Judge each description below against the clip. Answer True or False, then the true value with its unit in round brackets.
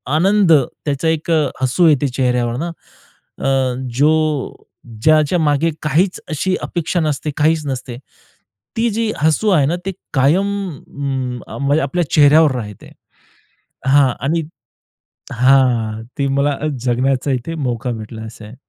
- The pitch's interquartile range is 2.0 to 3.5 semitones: False (4.0 semitones)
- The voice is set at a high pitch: False (140 Hz)